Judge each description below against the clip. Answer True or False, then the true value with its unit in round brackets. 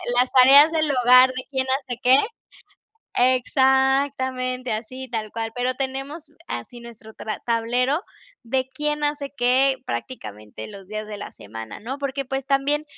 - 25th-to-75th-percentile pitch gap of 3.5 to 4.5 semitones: False (2.7 semitones)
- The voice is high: True (255 Hz)